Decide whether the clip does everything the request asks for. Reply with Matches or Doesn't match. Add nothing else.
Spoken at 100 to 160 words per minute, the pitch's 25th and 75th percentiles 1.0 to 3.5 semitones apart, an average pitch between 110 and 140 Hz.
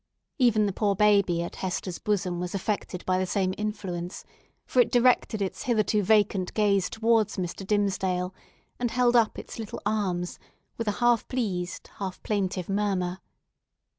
Doesn't match